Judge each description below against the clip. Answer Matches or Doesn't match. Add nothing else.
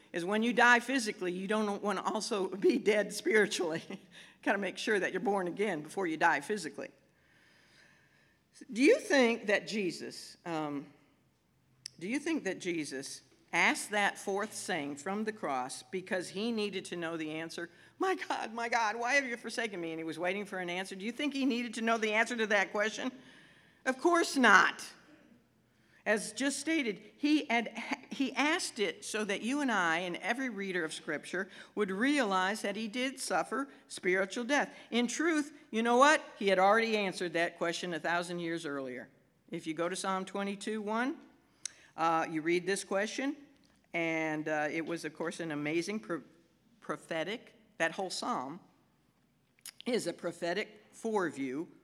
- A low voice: Doesn't match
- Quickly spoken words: Doesn't match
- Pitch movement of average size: Doesn't match